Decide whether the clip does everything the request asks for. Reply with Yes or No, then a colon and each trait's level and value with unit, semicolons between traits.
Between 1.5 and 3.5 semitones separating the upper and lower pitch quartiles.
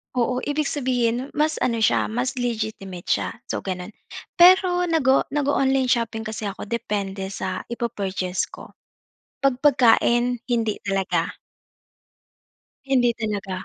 No: average, 4.8 semitones